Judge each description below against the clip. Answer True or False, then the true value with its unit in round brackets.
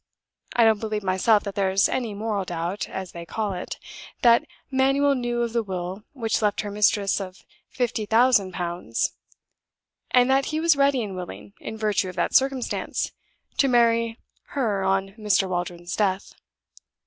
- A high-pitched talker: True (210 Hz)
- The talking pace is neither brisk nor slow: True (160 wpm)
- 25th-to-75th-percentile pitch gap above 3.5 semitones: True (4.1 semitones)